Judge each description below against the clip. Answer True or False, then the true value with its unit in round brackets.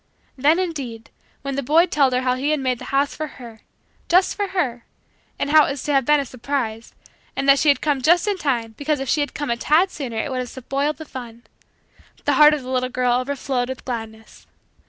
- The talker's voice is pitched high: True (275 Hz)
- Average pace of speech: False (225 wpm)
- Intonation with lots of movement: False (3.1 semitones)